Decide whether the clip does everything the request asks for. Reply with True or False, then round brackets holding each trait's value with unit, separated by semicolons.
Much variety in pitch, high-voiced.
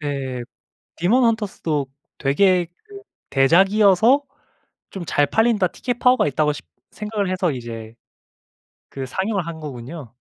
False (7.2 semitones; 175 Hz)